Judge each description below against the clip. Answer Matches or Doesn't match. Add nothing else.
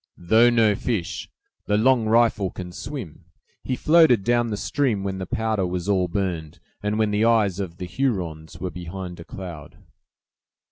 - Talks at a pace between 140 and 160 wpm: Doesn't match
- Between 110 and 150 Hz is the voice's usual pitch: Doesn't match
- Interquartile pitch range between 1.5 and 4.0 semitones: Doesn't match